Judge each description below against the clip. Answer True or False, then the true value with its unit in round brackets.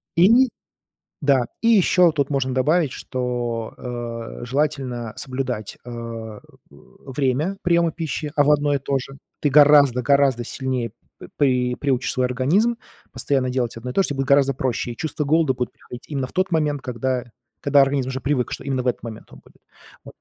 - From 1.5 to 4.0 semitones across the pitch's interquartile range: True (2.9 semitones)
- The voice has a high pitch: False (135 Hz)